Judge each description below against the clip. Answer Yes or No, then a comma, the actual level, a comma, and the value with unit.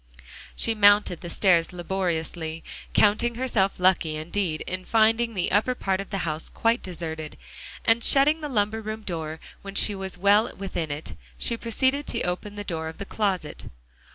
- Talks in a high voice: Yes, high, 195 Hz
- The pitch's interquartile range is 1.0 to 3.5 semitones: No, average, 4.5 semitones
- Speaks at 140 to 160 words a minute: No, average, 175 wpm